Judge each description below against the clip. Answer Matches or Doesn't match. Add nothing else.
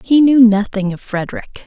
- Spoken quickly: Doesn't match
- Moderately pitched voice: Doesn't match